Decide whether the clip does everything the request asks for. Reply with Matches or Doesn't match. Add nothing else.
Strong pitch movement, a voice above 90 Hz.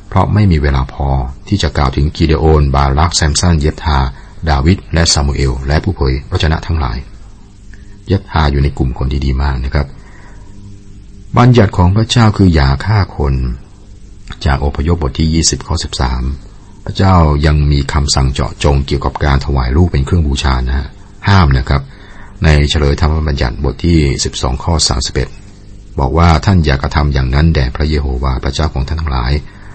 Doesn't match